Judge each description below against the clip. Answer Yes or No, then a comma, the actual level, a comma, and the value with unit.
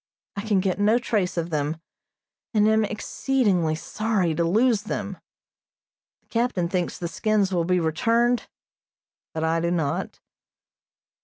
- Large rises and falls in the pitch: No, average, 4.5 semitones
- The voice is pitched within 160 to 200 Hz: Yes, high, 190 Hz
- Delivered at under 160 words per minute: Yes, average, 140 wpm